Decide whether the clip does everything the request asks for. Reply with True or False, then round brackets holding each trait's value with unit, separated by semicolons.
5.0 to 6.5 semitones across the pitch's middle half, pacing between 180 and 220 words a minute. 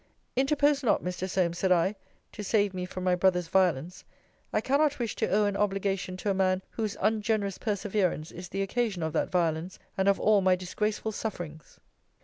False (2.7 semitones; 185 wpm)